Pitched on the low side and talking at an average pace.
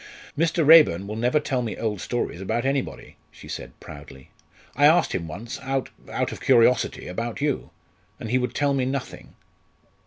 Yes: low, 125 Hz; average, 175 wpm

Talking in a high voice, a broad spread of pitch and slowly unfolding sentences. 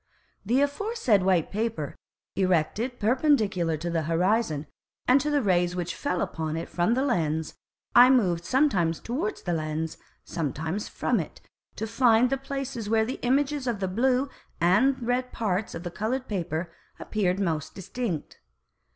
No: high, 210 Hz; wide, 6.7 semitones; average, 155 wpm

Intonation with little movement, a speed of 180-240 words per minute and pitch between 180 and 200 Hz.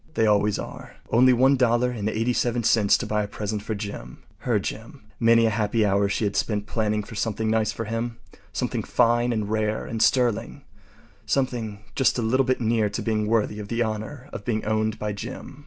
No: narrow, 2.0 semitones; average, 185 wpm; low, 110 Hz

